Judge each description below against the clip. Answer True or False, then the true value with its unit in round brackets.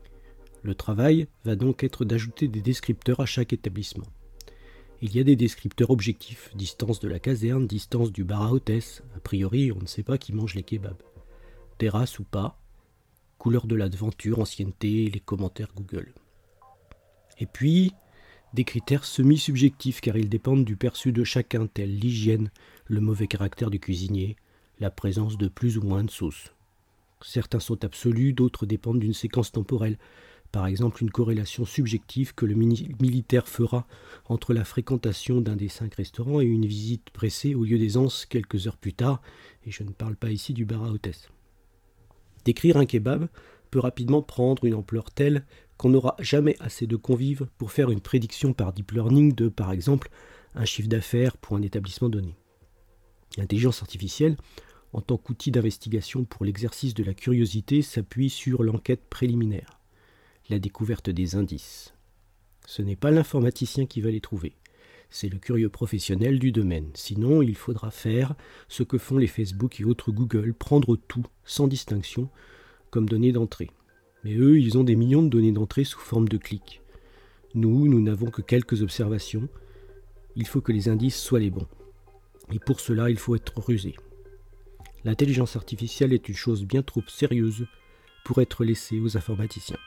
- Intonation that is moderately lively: True (3.5 semitones)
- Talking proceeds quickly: False (165 wpm)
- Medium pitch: False (115 Hz)